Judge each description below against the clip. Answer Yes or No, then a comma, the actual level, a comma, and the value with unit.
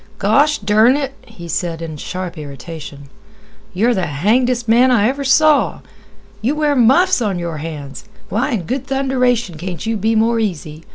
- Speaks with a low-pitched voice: No, high, 220 Hz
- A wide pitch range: Yes, wide, 7.1 semitones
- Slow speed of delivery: No, average, 165 wpm